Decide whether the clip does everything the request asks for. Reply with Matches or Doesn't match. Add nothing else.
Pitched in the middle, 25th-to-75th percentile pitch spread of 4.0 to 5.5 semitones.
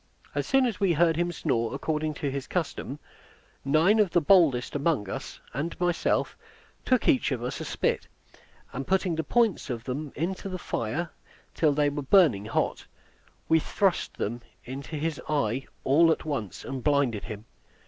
Matches